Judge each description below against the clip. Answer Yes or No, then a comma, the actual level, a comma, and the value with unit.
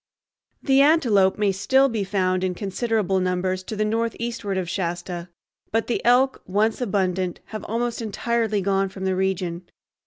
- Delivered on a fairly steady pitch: No, average, 3.6 semitones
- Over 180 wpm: No, average, 155 wpm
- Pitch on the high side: Yes, high, 200 Hz